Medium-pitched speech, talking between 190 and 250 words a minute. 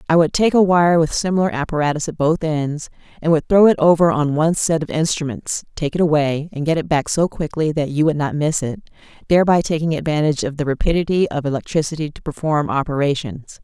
Yes: medium, 155 Hz; fast, 205 wpm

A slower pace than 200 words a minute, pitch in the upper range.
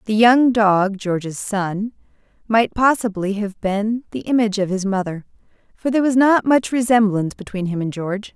Yes: average, 170 wpm; high, 210 Hz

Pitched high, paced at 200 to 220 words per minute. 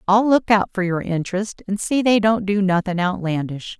Yes: high, 195 Hz; fast, 205 wpm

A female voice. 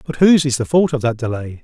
No: male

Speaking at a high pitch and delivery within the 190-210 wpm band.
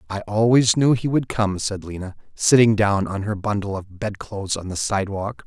No: low, 105 Hz; average, 200 wpm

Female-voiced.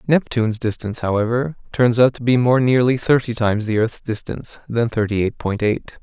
No: male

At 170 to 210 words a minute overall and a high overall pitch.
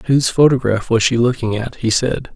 No: fast, 205 wpm; low, 120 Hz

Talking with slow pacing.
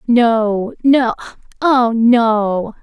Yes: slow, 65 wpm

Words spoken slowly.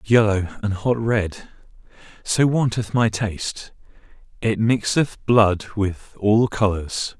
Yes: slow, 110 wpm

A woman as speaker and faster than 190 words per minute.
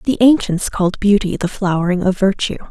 No: female; average, 175 wpm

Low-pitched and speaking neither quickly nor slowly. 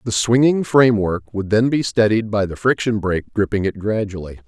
Yes: low, 110 Hz; average, 190 wpm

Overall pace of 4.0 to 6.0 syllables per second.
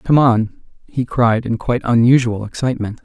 Yes: 5.1 syllables/s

